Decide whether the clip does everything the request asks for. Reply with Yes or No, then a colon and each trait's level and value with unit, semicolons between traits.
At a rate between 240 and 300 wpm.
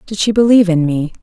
Yes: fast, 245 wpm